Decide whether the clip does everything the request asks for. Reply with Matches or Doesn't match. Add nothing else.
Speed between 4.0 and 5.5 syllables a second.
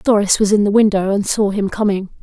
Doesn't match